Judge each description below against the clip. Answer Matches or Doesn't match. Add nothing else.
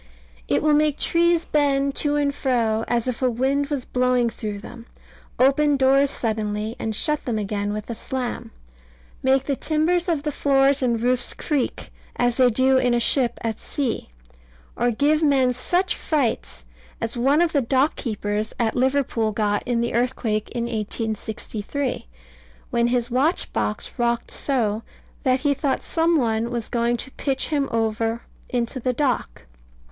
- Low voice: Doesn't match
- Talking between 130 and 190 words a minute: Matches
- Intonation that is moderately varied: Matches